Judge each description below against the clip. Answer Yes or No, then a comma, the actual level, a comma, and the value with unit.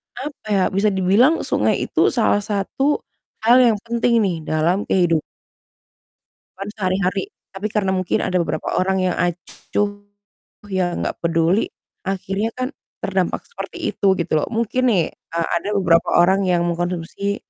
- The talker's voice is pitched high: Yes, high, 195 Hz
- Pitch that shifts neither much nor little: Yes, average, 3.1 semitones